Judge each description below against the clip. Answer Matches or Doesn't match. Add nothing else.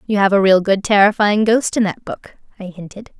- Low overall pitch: Doesn't match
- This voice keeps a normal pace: Doesn't match